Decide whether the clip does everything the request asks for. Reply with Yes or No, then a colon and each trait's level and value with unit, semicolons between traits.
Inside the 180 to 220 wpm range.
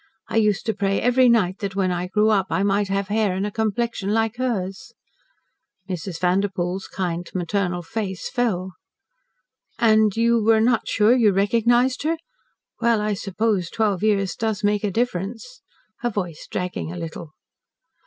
No: average, 160 wpm